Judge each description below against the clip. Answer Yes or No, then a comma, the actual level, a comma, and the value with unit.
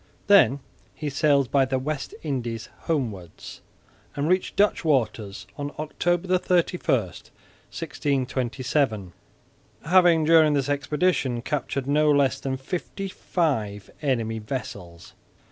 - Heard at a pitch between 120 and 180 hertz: Yes, medium, 140 Hz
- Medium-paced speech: No, slow, 110 wpm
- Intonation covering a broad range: No, average, 4.4 semitones